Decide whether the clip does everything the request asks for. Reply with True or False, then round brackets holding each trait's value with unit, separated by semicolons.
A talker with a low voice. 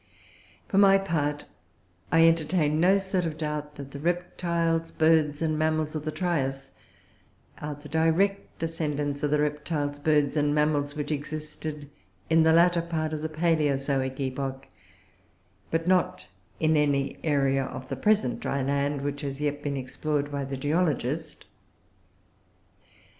False (150 Hz)